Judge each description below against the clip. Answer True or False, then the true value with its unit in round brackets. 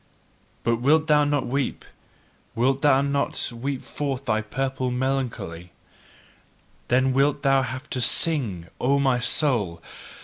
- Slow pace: True (130 wpm)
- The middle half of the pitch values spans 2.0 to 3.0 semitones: True (2.5 semitones)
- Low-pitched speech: True (130 Hz)